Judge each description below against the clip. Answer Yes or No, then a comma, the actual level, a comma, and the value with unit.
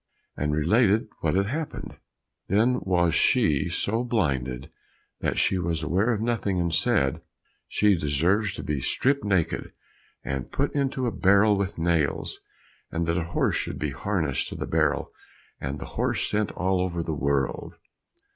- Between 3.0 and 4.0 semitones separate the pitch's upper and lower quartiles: No, wide, 5.5 semitones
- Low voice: Yes, very low, 90 Hz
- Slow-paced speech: No, average, 160 wpm